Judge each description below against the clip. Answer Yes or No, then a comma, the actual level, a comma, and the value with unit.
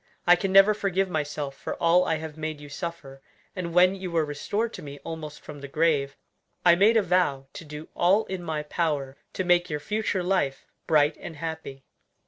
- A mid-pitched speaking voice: Yes, medium, 165 Hz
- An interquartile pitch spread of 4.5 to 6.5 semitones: No, average, 3.6 semitones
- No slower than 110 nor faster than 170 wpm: No, average, 200 wpm